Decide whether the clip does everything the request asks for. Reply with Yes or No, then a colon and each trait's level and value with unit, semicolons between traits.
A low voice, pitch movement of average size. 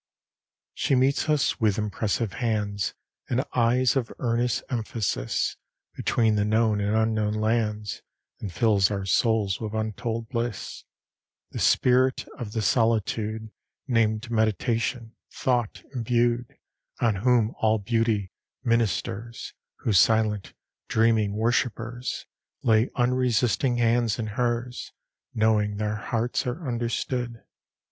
No: low, 115 Hz; narrow, 2.1 semitones